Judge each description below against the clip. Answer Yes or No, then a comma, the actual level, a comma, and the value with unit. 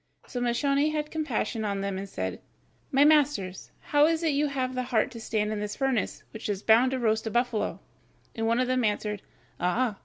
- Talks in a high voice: Yes, high, 240 Hz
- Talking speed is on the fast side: Yes, fast, 210 wpm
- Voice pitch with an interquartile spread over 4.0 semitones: Yes, average, 4.7 semitones